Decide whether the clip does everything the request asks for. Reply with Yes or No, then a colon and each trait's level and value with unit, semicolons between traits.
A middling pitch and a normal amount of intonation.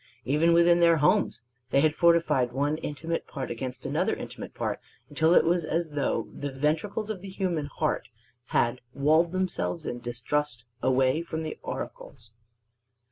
Yes: medium, 150 Hz; average, 4.2 semitones